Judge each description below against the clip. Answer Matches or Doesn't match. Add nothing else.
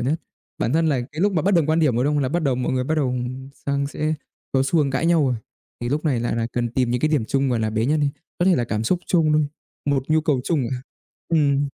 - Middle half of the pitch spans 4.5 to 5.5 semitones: Doesn't match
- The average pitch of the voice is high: Doesn't match